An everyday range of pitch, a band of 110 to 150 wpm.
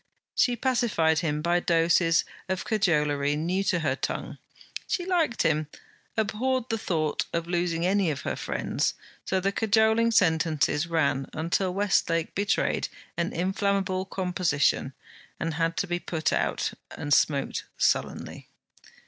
Yes: average, 3.9 semitones; slow, 135 wpm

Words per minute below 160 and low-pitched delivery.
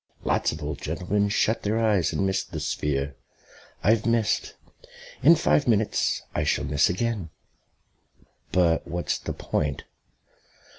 Yes: slow, 135 wpm; very low, 95 Hz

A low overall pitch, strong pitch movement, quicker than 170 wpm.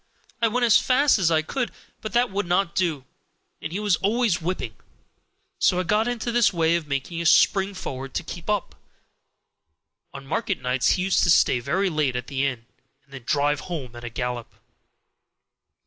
No: medium, 170 Hz; wide, 6.8 semitones; average, 190 wpm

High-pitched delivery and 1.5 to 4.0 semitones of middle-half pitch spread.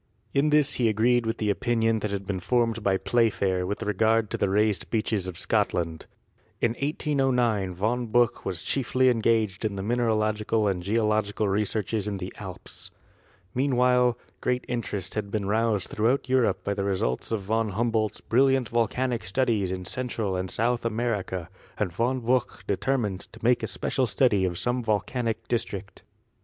No: low, 110 Hz; average, 3.3 semitones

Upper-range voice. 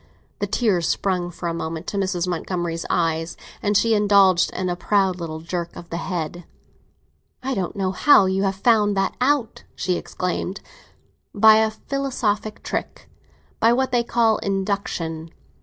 Yes: high, 195 Hz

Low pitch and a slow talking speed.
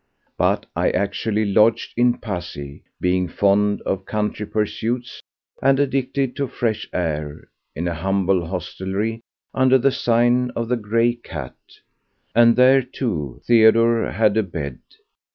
Yes: low, 110 Hz; slow, 125 wpm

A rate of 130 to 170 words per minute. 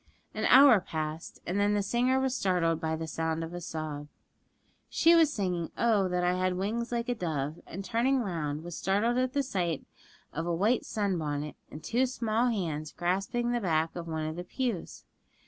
No: average, 200 wpm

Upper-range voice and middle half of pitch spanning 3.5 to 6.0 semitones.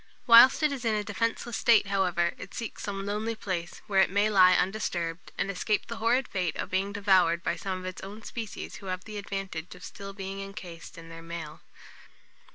No: high, 195 Hz; average, 3.0 semitones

